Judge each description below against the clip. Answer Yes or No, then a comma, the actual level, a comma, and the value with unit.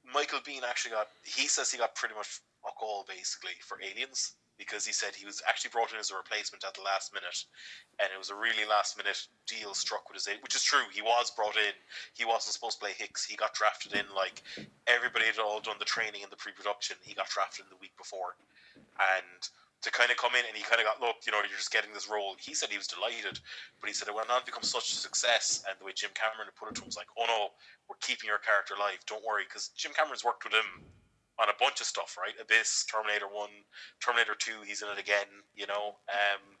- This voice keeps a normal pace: No, fast, 255 wpm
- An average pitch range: No, narrow, 1.5 semitones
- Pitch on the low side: Yes, low, 105 Hz